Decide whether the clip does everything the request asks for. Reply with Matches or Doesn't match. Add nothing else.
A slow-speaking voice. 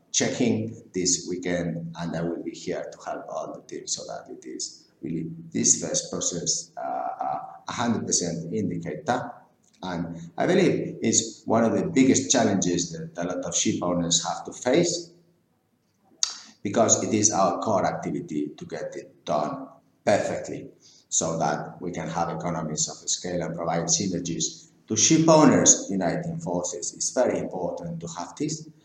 Doesn't match